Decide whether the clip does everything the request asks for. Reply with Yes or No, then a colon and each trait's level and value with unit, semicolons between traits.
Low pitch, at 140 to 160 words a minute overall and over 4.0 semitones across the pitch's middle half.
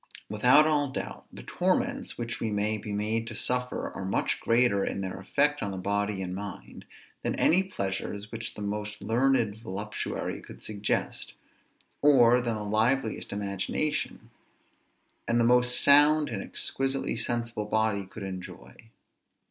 No: low, 110 Hz; average, 150 wpm; average, 3.5 semitones